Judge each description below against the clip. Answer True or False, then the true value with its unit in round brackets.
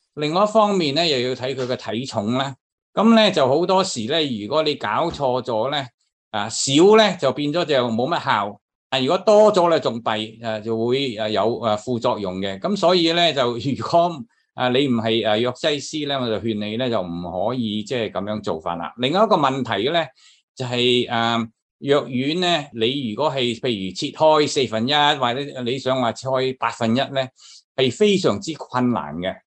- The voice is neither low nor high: False (130 Hz)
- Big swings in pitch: False (4.7 semitones)